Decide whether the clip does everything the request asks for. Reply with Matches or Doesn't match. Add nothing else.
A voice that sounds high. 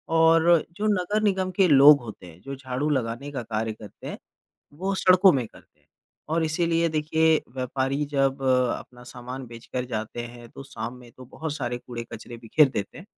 Doesn't match